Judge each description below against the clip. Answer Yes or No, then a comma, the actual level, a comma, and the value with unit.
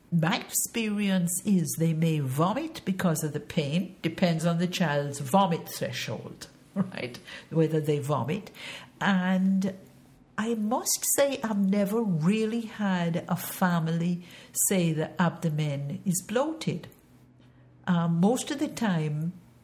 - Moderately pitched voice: Yes, medium, 180 Hz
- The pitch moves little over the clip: No, average, 3.6 semitones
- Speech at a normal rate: No, slow, 120 wpm